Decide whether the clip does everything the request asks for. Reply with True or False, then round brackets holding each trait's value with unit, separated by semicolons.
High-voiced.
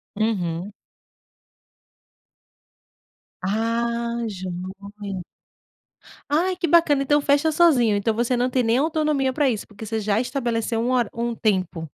True (235 Hz)